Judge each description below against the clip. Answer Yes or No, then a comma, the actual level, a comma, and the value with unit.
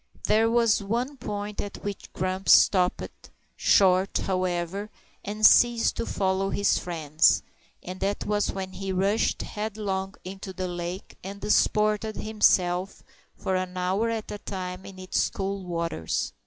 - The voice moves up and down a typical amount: No, narrow, 2.2 semitones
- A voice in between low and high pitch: No, high, 195 Hz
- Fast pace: No, average, 140 wpm